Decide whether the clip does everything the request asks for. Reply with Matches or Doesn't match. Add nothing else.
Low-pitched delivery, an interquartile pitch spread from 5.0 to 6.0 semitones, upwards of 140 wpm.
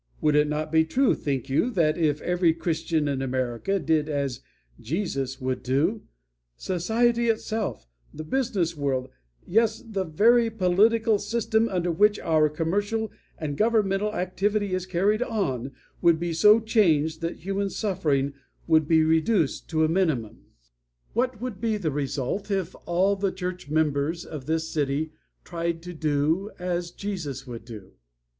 Doesn't match